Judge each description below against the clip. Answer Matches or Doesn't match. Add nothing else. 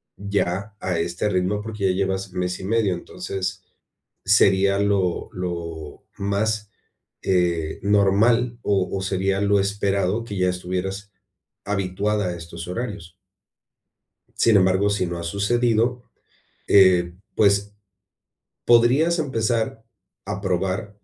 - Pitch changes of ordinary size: Doesn't match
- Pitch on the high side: Doesn't match